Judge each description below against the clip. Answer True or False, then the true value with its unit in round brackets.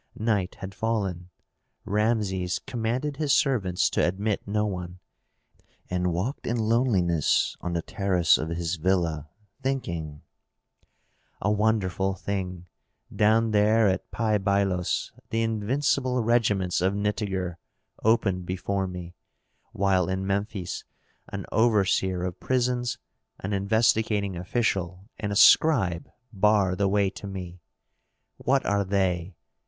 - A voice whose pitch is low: True (100 Hz)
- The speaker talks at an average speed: False (120 wpm)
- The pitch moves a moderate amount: True (3.4 semitones)